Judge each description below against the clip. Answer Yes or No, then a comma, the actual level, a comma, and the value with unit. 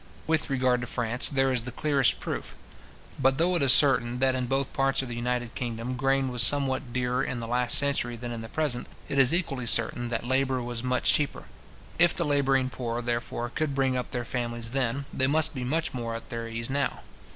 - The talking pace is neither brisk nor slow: No, fast, 220 wpm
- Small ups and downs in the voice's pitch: Yes, narrow, 2.2 semitones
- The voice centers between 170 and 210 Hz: No, low, 125 Hz